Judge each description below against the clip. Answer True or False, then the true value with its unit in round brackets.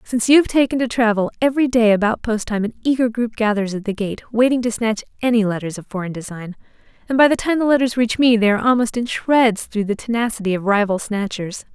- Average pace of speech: False (230 wpm)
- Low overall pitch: False (225 Hz)